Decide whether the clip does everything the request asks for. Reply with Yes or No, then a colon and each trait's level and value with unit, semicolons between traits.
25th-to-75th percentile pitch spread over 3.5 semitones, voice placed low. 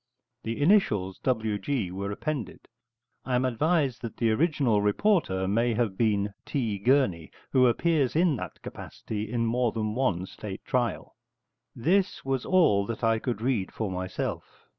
Yes: average, 4.7 semitones; low, 115 Hz